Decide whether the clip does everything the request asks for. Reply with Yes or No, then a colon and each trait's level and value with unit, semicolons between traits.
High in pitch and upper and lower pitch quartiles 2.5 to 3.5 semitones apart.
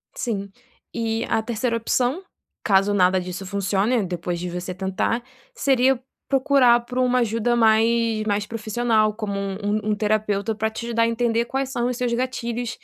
Yes: high, 225 Hz; average, 2.8 semitones